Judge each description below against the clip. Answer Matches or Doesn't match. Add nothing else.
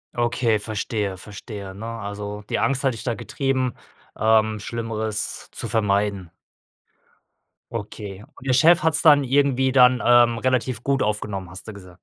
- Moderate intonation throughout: Matches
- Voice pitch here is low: Matches